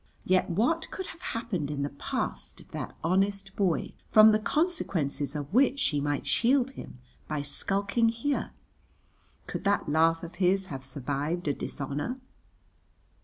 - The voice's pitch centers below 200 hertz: Yes, medium, 185 Hz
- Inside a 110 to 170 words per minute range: Yes, average, 150 wpm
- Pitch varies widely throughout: Yes, wide, 7.7 semitones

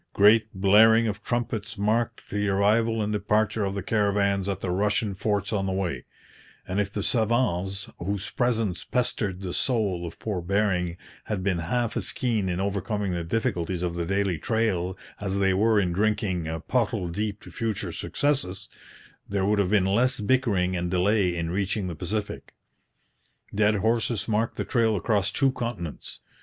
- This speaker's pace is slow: No, average, 170 wpm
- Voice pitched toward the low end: Yes, low, 100 Hz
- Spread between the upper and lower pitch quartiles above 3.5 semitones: No, average, 2.9 semitones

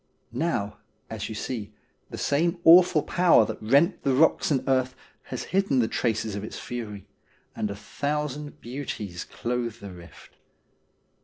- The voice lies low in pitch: Yes, low, 125 Hz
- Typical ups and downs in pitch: No, wide, 5.8 semitones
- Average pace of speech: Yes, average, 150 wpm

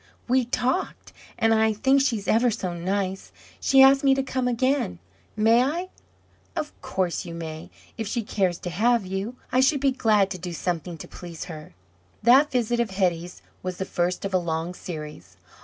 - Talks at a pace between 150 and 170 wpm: No, average, 185 wpm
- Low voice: No, high, 205 Hz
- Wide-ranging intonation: Yes, wide, 6.1 semitones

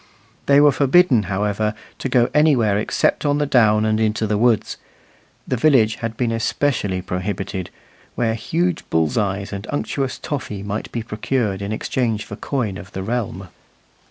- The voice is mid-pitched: No, low, 110 Hz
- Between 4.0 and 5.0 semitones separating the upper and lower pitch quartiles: Yes, average, 4.3 semitones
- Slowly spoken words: No, average, 160 wpm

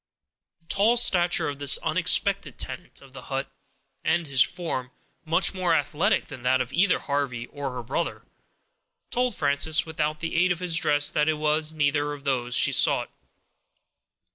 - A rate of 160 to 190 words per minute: Yes, average, 165 wpm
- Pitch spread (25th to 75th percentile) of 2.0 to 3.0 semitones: No, average, 3.4 semitones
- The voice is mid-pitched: Yes, medium, 150 Hz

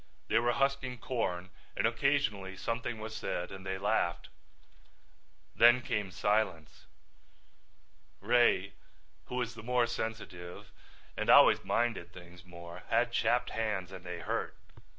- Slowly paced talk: Yes, slow, 130 wpm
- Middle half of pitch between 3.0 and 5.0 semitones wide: Yes, average, 4.6 semitones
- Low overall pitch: Yes, low, 110 Hz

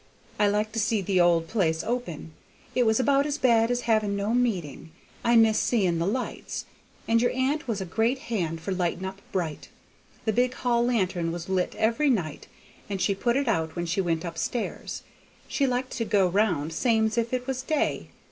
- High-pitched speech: Yes, high, 215 Hz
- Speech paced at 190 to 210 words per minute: Yes, average, 200 wpm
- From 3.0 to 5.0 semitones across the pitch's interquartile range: No, wide, 5.4 semitones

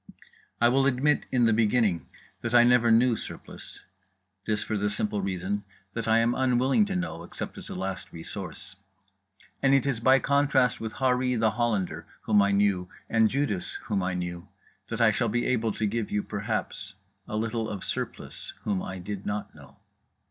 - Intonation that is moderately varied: Yes, average, 3.7 semitones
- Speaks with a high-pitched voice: No, low, 110 Hz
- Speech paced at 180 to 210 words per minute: Yes, average, 185 wpm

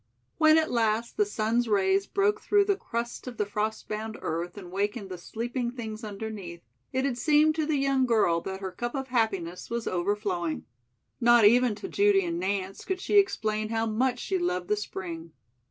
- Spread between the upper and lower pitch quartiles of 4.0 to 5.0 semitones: Yes, average, 4.4 semitones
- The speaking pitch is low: No, high, 220 Hz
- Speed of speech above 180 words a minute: Yes, average, 190 wpm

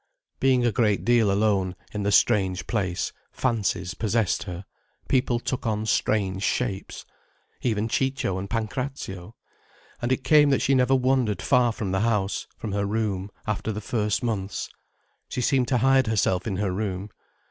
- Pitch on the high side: No, low, 110 Hz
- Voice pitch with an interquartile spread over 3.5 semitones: Yes, average, 4.0 semitones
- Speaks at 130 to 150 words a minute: No, average, 160 wpm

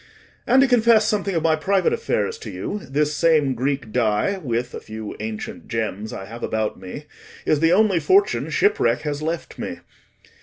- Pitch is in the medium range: Yes, medium, 155 Hz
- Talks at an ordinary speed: Yes, average, 180 wpm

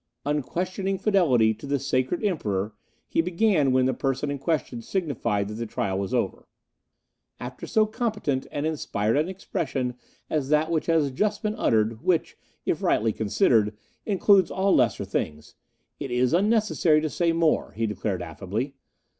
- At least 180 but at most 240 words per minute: No, average, 160 wpm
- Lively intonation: Yes, wide, 7.9 semitones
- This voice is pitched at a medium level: Yes, medium, 145 Hz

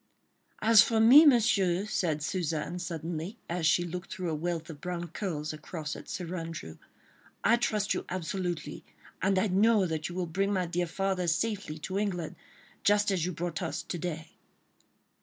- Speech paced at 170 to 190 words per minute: Yes, average, 175 wpm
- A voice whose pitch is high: No, medium, 180 Hz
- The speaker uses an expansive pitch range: No, average, 3.2 semitones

